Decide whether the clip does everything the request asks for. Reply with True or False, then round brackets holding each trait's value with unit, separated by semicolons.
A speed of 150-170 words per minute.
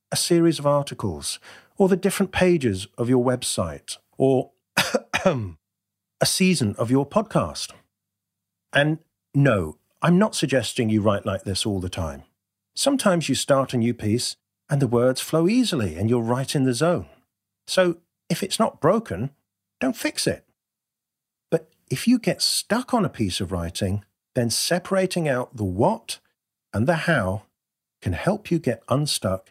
True (155 wpm)